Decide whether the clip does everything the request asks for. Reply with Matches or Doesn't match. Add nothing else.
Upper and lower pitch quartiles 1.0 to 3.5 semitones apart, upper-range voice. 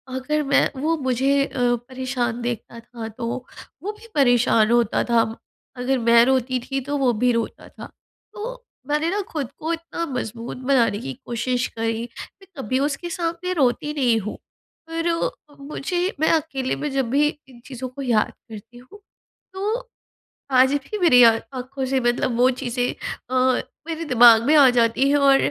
Doesn't match